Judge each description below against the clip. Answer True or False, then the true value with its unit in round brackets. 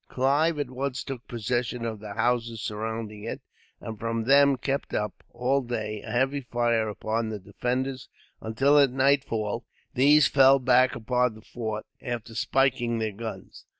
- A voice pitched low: True (120 Hz)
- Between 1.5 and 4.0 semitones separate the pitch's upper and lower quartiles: True (3.2 semitones)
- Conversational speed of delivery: True (155 wpm)